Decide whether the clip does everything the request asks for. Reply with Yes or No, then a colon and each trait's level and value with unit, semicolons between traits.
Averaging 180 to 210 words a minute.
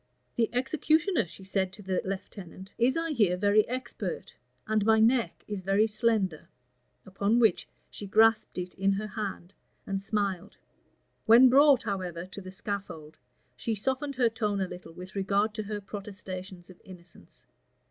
No: average, 155 wpm